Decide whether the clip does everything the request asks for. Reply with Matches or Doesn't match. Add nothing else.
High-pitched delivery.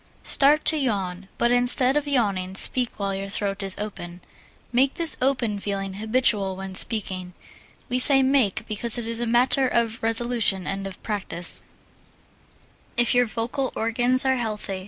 Matches